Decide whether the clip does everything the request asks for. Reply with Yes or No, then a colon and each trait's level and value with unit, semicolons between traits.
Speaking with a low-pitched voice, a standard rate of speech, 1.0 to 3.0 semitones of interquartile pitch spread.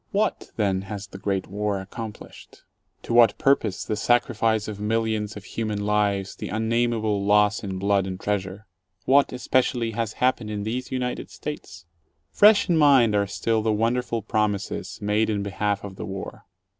Yes: low, 105 Hz; average, 170 wpm; narrow, 2.4 semitones